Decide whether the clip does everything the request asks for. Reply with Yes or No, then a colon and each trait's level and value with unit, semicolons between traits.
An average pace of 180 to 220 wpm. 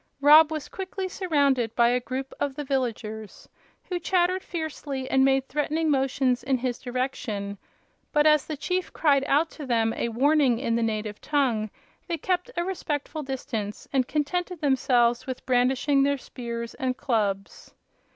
No: average, 160 wpm